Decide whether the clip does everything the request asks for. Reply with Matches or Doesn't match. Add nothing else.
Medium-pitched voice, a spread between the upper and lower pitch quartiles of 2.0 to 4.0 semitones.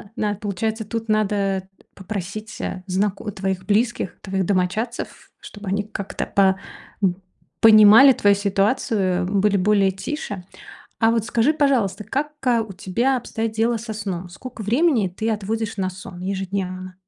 Doesn't match